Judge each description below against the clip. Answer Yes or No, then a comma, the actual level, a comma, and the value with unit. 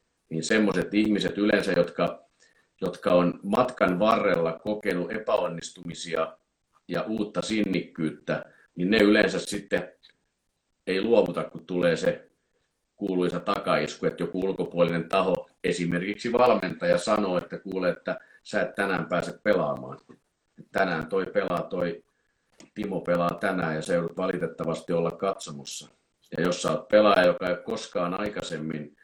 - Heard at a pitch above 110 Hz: No, very low, 85 Hz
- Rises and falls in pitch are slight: No, average, 3.5 semitones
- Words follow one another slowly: No, average, 130 wpm